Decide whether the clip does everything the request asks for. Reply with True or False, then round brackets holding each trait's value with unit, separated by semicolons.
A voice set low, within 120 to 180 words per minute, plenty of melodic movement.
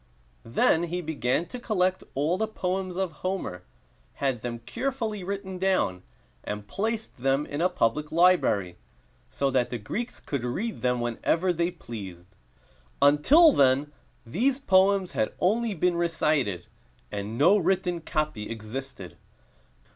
False (165 Hz; 135 wpm; 7.4 semitones)